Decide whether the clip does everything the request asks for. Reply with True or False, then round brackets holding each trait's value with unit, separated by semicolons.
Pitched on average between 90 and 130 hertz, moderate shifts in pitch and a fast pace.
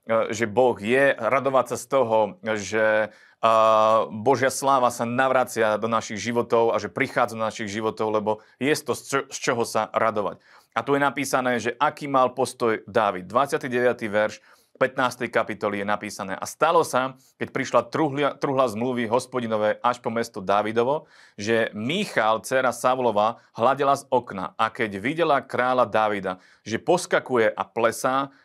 False (120 Hz; 3.1 semitones; 150 wpm)